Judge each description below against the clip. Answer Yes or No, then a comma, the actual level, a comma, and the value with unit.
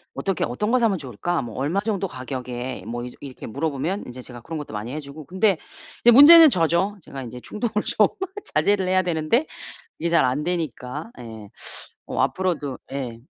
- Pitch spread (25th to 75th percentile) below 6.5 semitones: No, wide, 7.3 semitones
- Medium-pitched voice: Yes, medium, 155 Hz